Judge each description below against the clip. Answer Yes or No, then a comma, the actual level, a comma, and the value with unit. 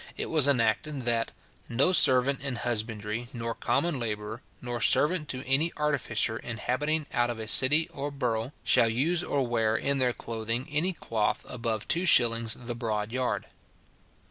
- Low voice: Yes, low, 120 Hz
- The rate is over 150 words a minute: Yes, average, 160 wpm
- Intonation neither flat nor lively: Yes, average, 3.7 semitones